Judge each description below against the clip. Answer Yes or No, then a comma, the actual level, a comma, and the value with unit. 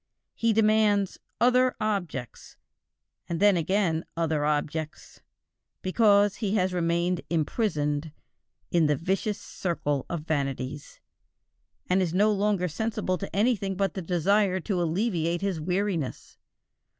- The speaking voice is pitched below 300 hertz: Yes, medium, 185 Hz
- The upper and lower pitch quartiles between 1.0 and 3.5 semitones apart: No, average, 4.2 semitones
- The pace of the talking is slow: Yes, slow, 120 wpm